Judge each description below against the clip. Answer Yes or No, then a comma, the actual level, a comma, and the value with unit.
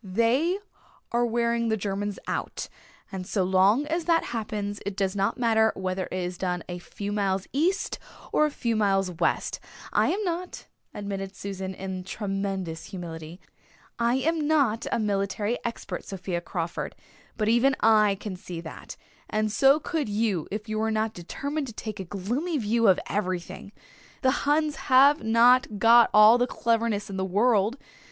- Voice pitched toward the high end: Yes, high, 210 Hz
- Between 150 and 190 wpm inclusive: Yes, average, 165 wpm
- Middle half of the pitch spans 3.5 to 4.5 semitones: Yes, average, 3.8 semitones